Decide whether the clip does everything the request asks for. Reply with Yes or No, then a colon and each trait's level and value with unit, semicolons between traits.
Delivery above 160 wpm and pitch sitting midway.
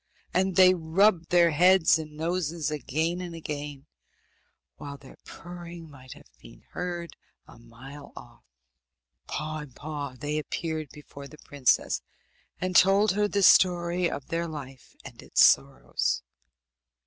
No: average, 140 wpm; medium, 160 Hz